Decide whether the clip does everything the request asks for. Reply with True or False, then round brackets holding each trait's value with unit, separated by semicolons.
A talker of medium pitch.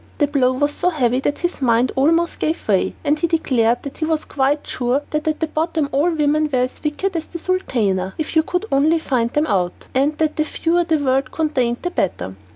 False (295 Hz)